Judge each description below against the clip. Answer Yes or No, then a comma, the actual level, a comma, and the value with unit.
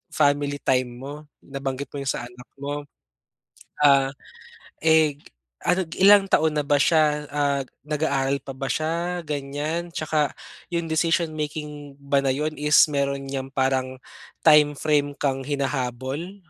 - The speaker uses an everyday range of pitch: No, narrow, 2.2 semitones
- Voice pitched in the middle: Yes, medium, 145 Hz